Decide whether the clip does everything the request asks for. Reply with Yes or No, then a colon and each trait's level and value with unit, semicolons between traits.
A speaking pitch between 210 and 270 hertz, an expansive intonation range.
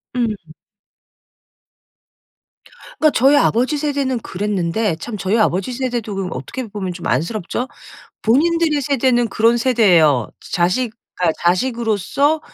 Yes: high, 230 Hz; wide, 5.9 semitones